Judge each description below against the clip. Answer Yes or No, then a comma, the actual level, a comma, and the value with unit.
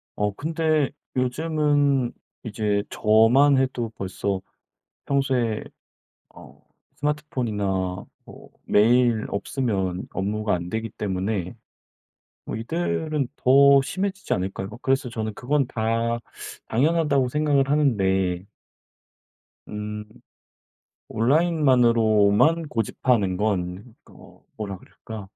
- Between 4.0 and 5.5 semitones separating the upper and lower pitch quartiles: Yes, average, 5.2 semitones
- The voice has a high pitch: No, low, 115 Hz